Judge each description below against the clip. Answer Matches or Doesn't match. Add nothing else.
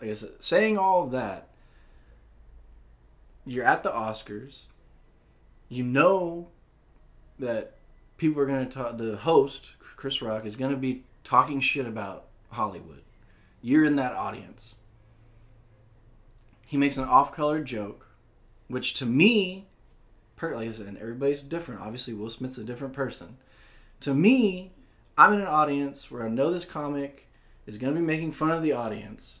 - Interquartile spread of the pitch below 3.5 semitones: Doesn't match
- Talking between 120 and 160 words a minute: Matches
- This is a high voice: Doesn't match